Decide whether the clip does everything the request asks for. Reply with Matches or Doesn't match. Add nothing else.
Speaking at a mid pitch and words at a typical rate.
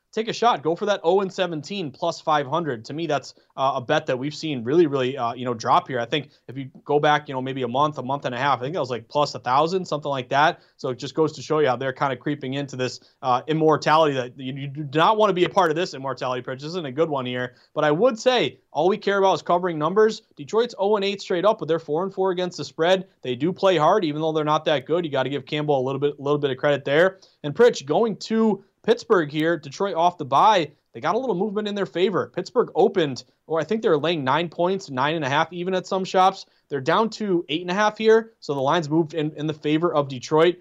Doesn't match